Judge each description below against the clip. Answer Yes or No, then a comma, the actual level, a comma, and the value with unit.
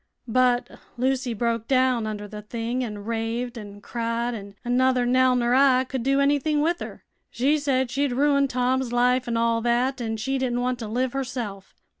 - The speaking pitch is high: Yes, high, 245 Hz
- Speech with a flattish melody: Yes, narrow, 2.1 semitones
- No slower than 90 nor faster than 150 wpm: No, average, 185 wpm